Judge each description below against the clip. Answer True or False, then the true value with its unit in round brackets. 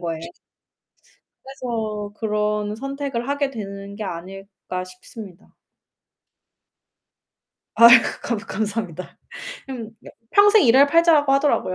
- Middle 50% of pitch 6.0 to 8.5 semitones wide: False (5.4 semitones)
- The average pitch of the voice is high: True (220 Hz)